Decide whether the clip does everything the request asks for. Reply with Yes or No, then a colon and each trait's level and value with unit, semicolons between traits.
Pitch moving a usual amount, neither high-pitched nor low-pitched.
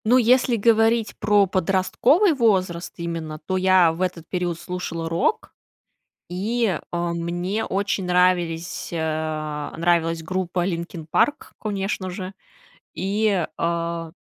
Yes: average, 3.3 semitones; medium, 180 Hz